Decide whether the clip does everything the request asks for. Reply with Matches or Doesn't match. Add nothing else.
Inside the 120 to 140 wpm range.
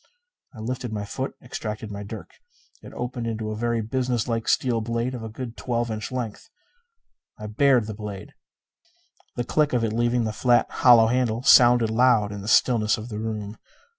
Doesn't match